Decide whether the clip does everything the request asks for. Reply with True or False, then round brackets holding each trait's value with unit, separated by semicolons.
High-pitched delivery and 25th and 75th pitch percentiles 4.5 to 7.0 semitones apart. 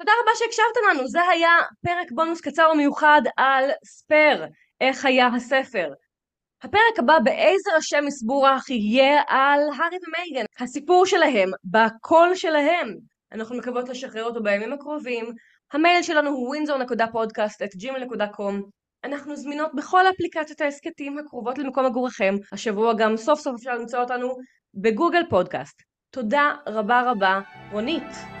True (275 Hz; 4.9 semitones)